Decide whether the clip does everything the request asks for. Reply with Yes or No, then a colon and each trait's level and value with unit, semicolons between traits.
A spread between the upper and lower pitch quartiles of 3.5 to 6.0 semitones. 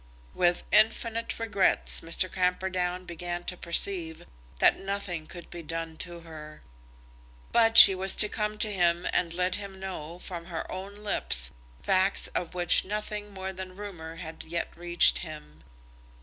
No: average, 2.7 semitones